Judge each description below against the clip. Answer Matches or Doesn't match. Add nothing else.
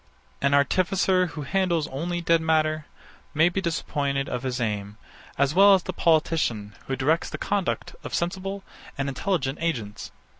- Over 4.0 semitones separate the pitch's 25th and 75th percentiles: Matches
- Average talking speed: Matches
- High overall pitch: Doesn't match